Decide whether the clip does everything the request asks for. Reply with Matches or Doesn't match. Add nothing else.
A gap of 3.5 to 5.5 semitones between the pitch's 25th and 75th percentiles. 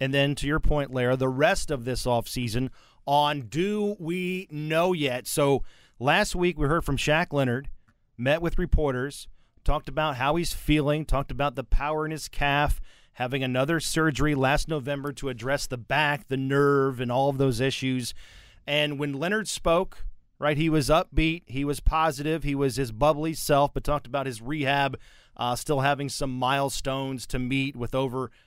Doesn't match